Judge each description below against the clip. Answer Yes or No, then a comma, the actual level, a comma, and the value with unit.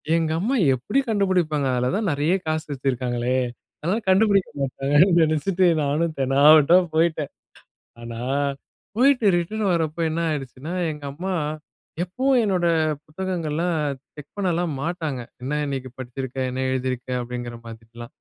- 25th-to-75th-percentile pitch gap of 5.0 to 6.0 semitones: Yes, average, 5.3 semitones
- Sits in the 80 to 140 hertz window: No, medium, 155 Hz